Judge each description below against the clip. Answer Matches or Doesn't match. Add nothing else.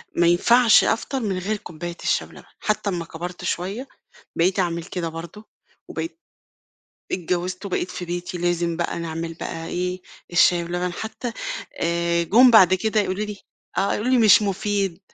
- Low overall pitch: Doesn't match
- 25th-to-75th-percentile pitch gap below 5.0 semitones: Matches